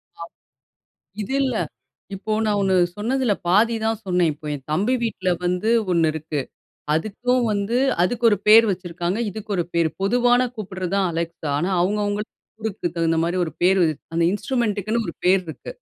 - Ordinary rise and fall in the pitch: Yes, average, 4.1 semitones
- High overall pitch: Yes, high, 195 Hz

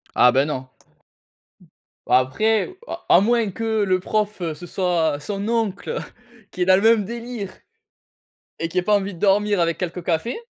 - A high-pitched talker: Yes, high, 195 Hz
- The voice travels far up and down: No, average, 4.2 semitones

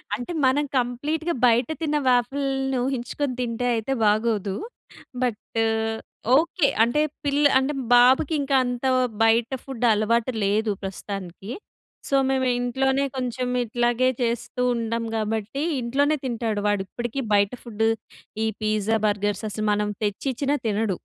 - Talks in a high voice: Yes, high, 240 Hz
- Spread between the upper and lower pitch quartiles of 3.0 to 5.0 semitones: Yes, average, 3.6 semitones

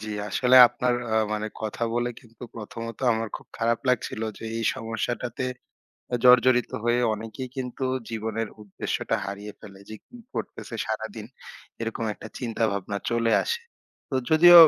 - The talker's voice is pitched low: Yes, low, 115 Hz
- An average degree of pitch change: No, narrow, 2.3 semitones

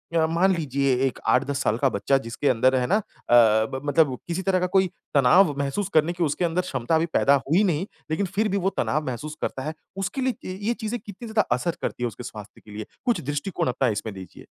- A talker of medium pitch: Yes, medium, 150 Hz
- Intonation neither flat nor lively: No, wide, 6.3 semitones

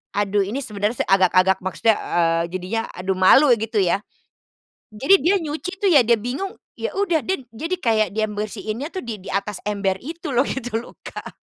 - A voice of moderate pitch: No, high, 220 Hz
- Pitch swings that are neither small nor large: No, wide, 6.5 semitones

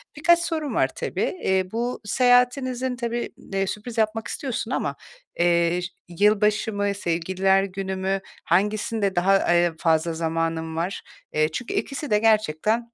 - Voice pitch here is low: No, high, 200 Hz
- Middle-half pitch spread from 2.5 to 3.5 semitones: No, average, 5.2 semitones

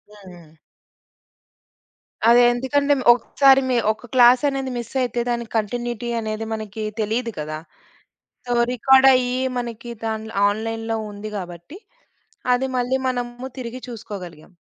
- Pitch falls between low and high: No, high, 235 Hz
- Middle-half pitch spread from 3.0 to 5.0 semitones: No, narrow, 2.6 semitones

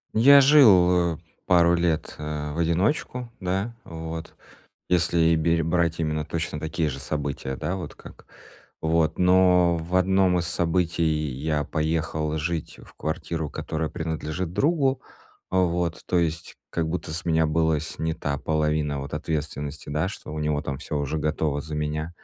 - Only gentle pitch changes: Yes, narrow, 2.3 semitones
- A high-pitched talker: No, very low, 80 Hz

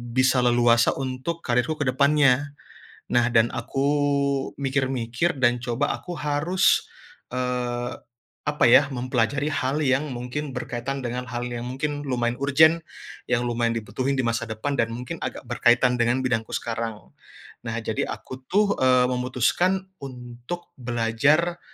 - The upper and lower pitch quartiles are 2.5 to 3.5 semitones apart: Yes, average, 2.9 semitones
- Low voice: Yes, low, 125 Hz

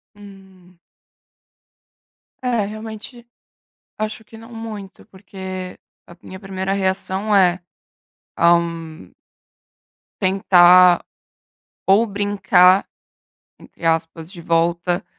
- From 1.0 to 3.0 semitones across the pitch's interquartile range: Yes, narrow, 2.6 semitones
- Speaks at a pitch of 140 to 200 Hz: Yes, high, 190 Hz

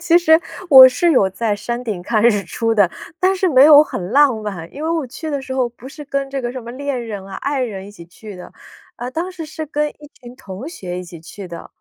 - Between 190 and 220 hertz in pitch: No, very high, 250 Hz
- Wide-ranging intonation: Yes, wide, 6.4 semitones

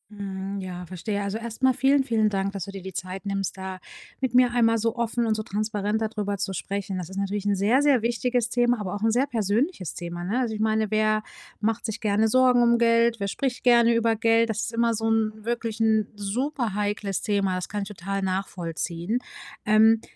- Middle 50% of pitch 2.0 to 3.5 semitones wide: Yes, average, 2.9 semitones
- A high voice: Yes, high, 215 Hz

